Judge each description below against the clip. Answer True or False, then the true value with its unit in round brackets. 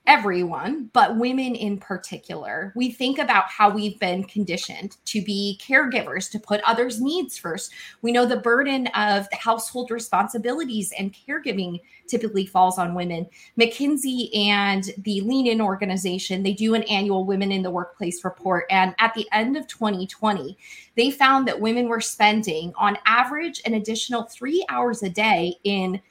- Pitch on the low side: False (210 Hz)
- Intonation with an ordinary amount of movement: True (3.7 semitones)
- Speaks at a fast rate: False (160 wpm)